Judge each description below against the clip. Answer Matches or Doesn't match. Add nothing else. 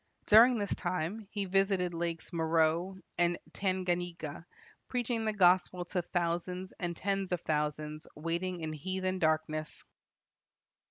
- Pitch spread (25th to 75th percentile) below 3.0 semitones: Matches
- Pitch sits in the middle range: Matches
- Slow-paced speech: Matches